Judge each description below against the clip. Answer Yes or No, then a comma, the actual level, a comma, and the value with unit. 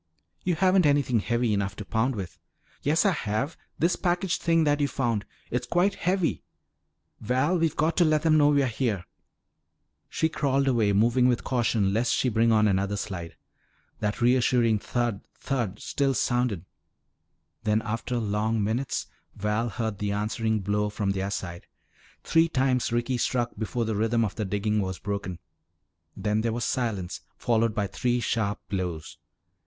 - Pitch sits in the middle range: No, low, 115 Hz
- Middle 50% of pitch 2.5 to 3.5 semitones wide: No, average, 4.2 semitones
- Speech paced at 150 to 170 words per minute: Yes, average, 160 wpm